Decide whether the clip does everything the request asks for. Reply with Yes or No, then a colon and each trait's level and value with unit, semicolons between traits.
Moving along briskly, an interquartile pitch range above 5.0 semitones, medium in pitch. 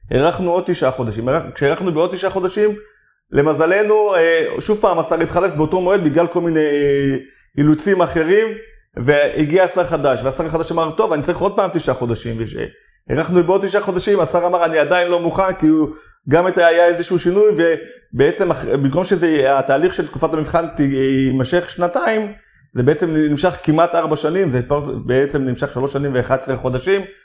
No: fast, 160 wpm; average, 4.5 semitones; medium, 165 Hz